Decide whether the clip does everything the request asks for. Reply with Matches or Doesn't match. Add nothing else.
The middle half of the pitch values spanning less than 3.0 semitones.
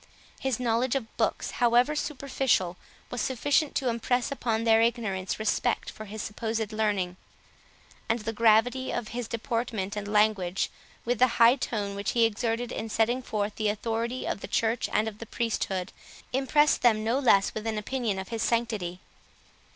Matches